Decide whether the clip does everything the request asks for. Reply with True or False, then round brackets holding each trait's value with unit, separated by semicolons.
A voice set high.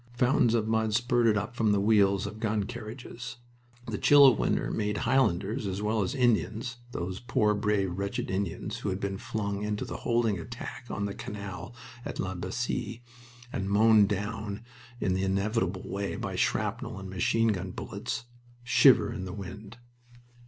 False (105 Hz)